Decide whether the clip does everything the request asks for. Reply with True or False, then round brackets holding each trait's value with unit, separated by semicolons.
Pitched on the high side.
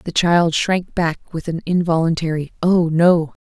False (170 Hz)